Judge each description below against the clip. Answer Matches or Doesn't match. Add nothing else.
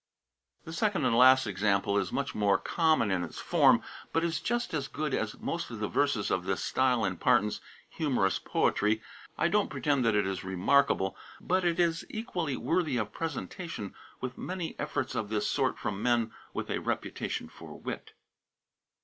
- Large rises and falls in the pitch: Matches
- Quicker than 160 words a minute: Matches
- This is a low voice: Matches